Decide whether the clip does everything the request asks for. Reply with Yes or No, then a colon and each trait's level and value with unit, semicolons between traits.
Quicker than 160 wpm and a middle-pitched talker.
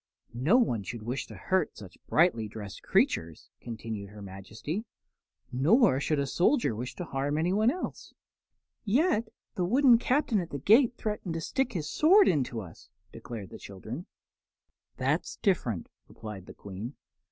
No: average, 155 wpm; medium, 145 Hz